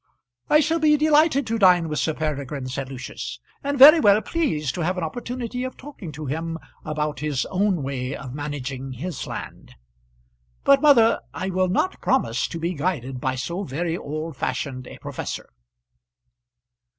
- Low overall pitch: No, medium, 165 Hz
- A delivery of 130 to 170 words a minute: Yes, average, 165 wpm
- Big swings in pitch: Yes, wide, 8.7 semitones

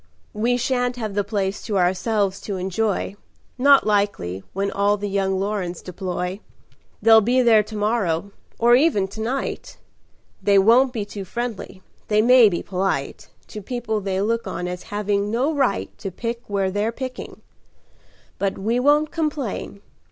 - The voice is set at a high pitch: Yes, high, 210 Hz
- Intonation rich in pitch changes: No, average, 3.5 semitones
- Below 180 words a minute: Yes, average, 160 wpm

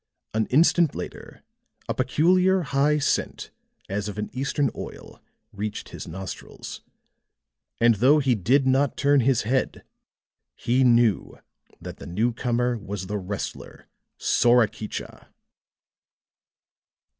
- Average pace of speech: No, slow, 110 wpm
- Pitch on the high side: No, low, 120 Hz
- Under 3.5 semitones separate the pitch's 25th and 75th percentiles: No, average, 4.5 semitones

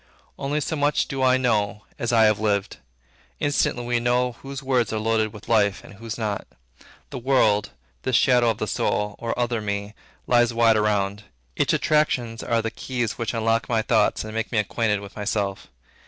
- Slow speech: No, average, 185 wpm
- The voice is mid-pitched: No, low, 115 Hz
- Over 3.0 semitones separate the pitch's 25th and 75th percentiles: No, narrow, 2.6 semitones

